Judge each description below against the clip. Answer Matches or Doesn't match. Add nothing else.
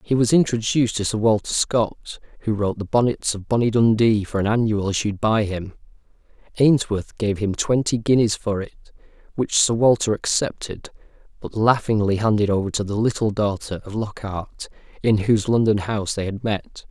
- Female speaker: Doesn't match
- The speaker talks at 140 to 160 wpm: Doesn't match